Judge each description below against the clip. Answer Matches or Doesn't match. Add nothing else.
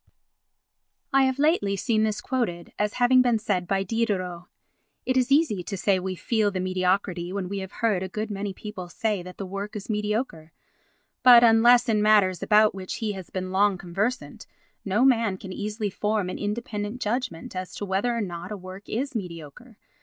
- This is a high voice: Matches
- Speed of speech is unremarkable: Matches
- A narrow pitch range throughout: Doesn't match